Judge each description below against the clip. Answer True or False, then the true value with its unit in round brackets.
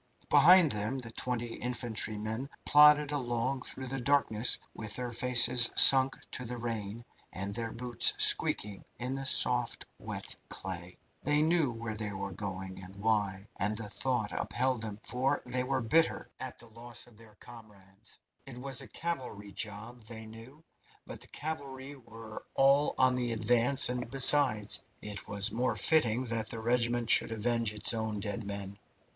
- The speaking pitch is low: True (120 Hz)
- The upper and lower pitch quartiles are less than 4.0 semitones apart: True (3.4 semitones)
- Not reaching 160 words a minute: False (165 wpm)